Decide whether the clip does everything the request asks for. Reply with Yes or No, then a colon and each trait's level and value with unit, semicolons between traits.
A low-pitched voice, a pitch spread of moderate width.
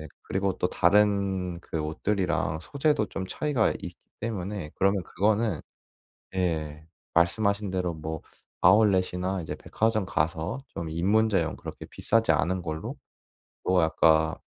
Yes: very low, 95 Hz; average, 4.1 semitones